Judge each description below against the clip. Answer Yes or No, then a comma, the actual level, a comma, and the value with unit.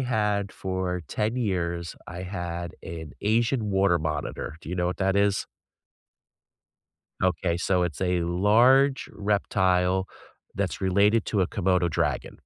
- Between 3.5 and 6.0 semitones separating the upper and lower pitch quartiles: No, average, 2.8 semitones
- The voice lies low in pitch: Yes, very low, 95 Hz